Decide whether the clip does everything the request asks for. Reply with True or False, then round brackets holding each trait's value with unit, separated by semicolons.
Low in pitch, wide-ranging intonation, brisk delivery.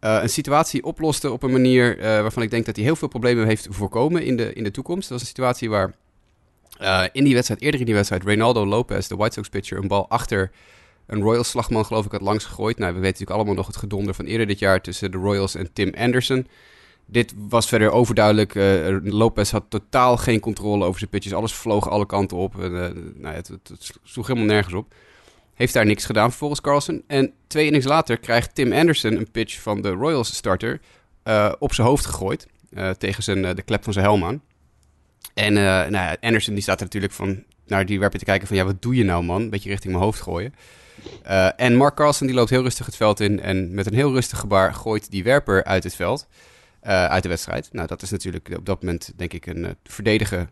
False (105 Hz; 3.6 semitones; 235 wpm)